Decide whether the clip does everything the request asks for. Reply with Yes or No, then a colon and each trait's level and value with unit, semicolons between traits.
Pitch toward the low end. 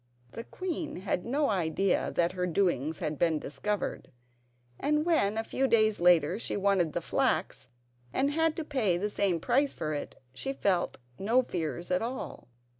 No: high, 200 Hz